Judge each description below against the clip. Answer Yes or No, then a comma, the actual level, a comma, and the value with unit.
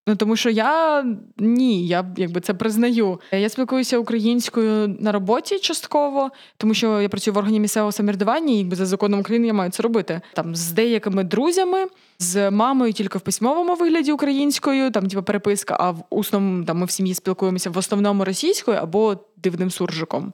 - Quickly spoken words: Yes, fast, 175 wpm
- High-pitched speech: Yes, high, 210 Hz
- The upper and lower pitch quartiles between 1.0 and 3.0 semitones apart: No, average, 3.6 semitones